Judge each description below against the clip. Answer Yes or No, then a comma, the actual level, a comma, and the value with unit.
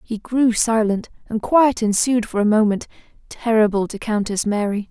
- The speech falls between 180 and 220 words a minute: No, average, 160 wpm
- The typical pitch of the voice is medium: No, high, 220 Hz